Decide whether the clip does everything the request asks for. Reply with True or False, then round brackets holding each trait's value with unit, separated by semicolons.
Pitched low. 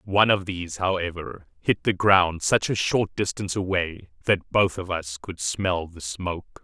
True (90 Hz)